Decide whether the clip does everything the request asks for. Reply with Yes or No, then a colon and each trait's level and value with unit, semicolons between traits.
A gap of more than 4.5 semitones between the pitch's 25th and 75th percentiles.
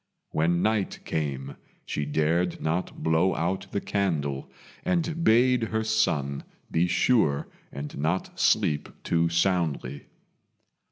Yes: wide, 5.4 semitones